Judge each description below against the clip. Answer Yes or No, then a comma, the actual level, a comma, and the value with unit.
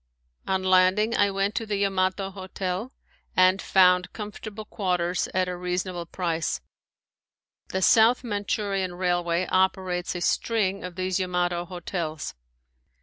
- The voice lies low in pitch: No, medium, 185 Hz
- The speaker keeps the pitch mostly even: Yes, narrow, 1.7 semitones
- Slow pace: Yes, slow, 125 wpm